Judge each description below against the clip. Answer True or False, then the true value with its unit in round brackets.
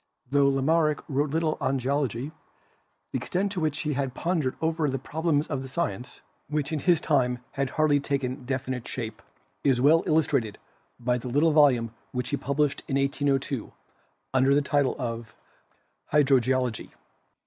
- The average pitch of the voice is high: False (140 Hz)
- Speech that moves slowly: False (160 wpm)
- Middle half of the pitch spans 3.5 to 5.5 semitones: False (2.8 semitones)